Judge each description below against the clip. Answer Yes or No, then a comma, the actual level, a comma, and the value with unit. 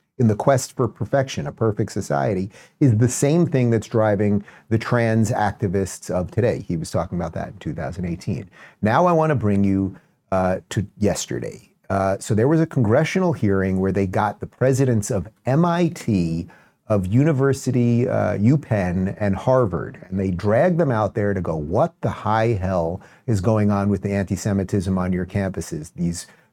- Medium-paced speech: Yes, average, 175 wpm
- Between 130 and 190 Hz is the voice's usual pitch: No, low, 105 Hz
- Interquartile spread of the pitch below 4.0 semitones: No, average, 4.9 semitones